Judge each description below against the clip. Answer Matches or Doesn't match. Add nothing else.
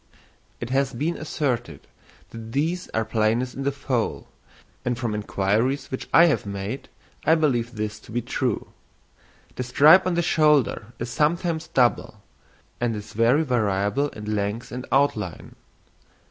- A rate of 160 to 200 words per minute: Doesn't match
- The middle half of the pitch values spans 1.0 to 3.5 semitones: Doesn't match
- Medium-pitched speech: Doesn't match